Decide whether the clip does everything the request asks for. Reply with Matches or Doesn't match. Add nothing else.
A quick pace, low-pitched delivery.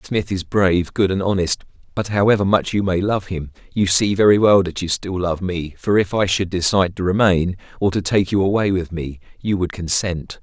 Matches